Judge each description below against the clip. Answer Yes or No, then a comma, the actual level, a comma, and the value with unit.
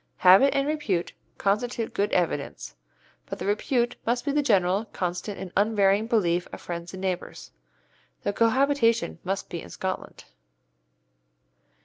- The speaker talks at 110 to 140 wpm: Yes, slow, 135 wpm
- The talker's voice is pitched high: Yes, high, 205 Hz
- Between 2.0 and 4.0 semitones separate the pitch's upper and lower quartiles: No, average, 4.5 semitones